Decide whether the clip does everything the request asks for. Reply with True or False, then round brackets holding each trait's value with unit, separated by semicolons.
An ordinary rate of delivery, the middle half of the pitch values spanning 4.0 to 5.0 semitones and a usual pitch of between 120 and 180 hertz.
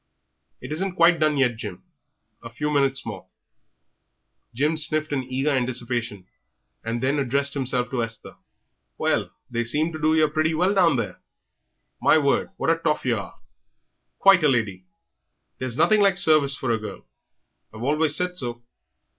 True (165 wpm; 4.7 semitones; 140 Hz)